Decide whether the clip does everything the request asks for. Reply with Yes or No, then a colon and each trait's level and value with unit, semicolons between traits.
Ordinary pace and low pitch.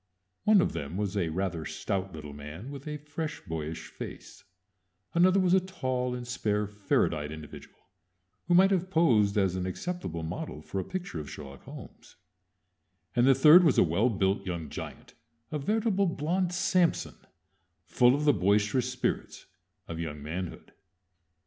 Yes: average, 160 wpm; low, 110 Hz